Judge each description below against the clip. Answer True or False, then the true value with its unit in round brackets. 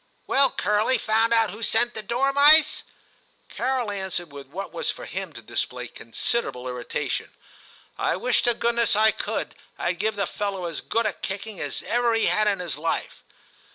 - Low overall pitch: False (215 Hz)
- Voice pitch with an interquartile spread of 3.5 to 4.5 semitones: True (4.2 semitones)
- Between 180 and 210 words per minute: True (185 wpm)